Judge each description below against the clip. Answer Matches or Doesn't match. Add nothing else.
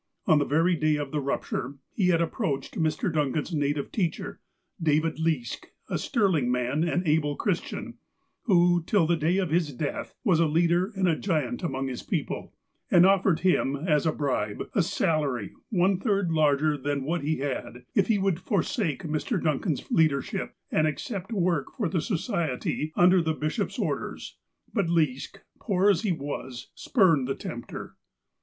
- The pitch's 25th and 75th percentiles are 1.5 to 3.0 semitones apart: Doesn't match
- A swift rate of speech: Doesn't match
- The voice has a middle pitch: Matches